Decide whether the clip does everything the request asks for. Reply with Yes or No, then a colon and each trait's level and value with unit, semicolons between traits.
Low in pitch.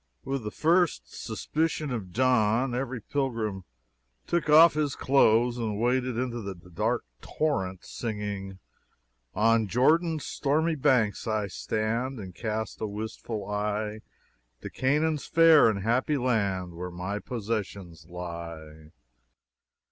Yes: low, 110 Hz